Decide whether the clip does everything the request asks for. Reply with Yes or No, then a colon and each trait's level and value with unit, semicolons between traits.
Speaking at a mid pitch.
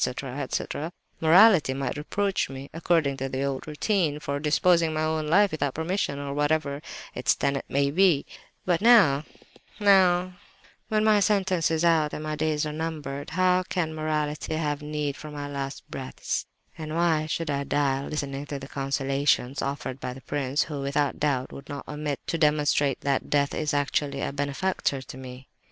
Yes: medium, 150 Hz